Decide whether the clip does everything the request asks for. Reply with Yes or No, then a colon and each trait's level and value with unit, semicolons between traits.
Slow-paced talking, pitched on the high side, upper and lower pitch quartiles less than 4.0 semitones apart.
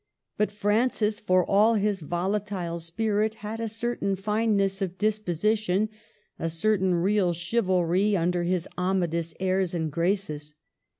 Yes: slow, 125 wpm; high, 195 Hz; average, 3.4 semitones